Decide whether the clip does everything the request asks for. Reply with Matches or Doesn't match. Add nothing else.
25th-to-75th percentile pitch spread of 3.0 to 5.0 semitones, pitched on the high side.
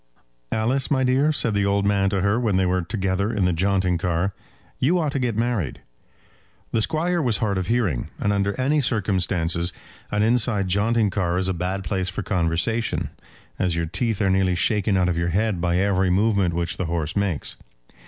Doesn't match